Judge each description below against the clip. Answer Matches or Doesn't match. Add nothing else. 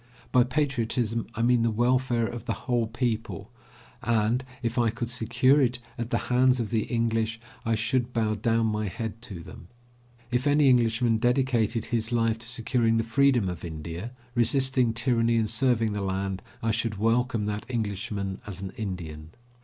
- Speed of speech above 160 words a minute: Matches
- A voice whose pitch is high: Doesn't match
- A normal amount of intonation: Doesn't match